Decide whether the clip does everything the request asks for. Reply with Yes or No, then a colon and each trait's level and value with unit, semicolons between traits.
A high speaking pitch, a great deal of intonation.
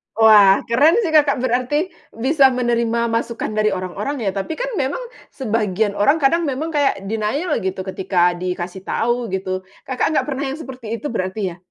Yes: high, 235 Hz; wide, 6.1 semitones